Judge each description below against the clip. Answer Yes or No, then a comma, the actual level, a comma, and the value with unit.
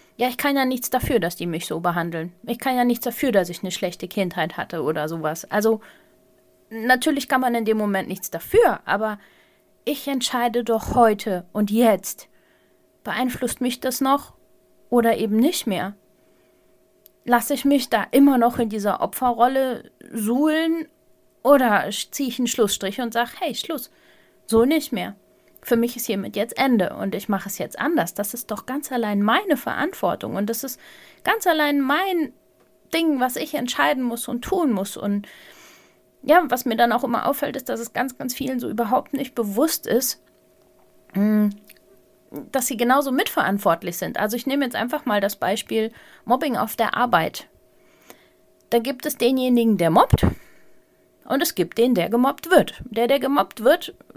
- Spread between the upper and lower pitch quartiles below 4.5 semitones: No, average, 4.8 semitones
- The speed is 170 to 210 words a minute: Yes, average, 175 wpm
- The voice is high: Yes, high, 240 Hz